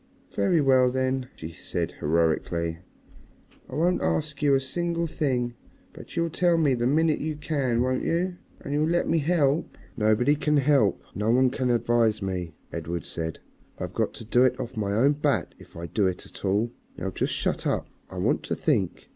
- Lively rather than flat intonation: Yes, wide, 6.2 semitones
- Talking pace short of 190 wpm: No, average, 195 wpm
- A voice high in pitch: No, low, 130 Hz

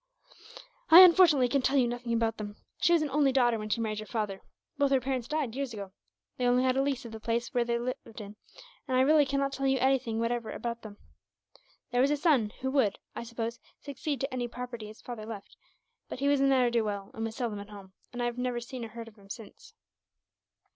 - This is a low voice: No, high, 245 Hz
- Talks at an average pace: No, fast, 235 wpm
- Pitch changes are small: No, average, 3.2 semitones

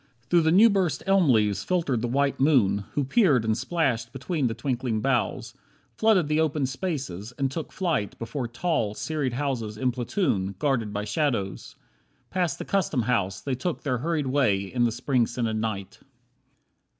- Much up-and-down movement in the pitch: Yes, wide, 5.7 semitones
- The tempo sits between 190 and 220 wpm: No, average, 165 wpm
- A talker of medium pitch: No, low, 130 Hz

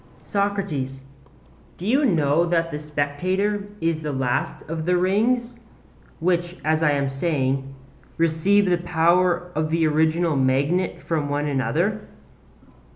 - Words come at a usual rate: No, slow, 130 wpm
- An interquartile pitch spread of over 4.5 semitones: No, average, 3.8 semitones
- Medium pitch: Yes, medium, 165 Hz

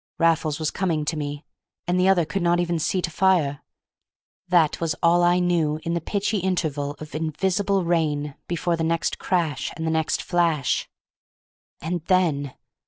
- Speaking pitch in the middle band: Yes, medium, 165 Hz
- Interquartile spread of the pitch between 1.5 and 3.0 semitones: Yes, narrow, 2.5 semitones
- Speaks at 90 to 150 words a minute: No, average, 170 wpm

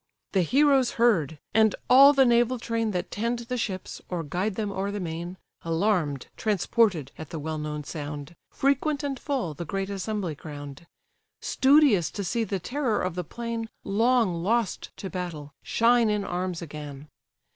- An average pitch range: No, wide, 6.1 semitones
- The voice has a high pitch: Yes, high, 195 Hz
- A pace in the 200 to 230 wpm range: No, average, 165 wpm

